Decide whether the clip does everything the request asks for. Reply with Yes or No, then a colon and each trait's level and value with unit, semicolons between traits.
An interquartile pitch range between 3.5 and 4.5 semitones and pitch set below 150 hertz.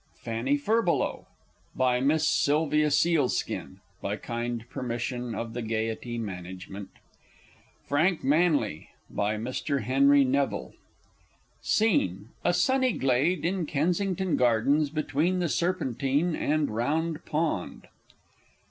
No: wide, 5.6 semitones; medium, 140 Hz